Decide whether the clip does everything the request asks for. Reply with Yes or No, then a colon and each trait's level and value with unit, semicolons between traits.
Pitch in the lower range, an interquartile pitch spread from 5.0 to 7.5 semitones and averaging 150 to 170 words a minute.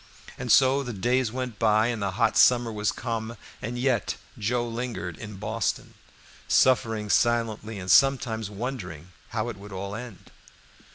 No: low, 115 Hz; average, 2.8 semitones; average, 155 wpm